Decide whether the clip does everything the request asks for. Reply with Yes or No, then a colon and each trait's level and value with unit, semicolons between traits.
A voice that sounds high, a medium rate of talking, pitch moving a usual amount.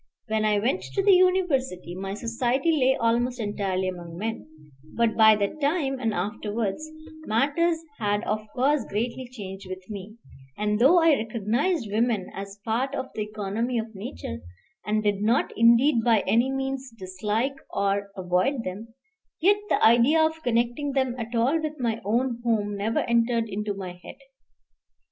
Yes: high, 230 Hz; average, 160 wpm; average, 4.3 semitones